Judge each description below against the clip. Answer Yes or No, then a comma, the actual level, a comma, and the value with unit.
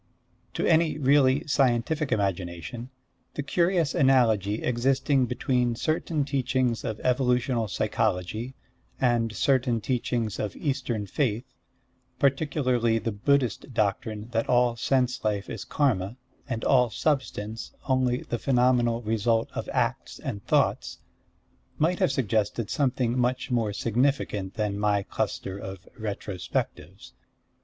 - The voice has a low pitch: Yes, low, 120 Hz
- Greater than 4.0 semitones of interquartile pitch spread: No, average, 3.6 semitones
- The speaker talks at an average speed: No, slow, 115 wpm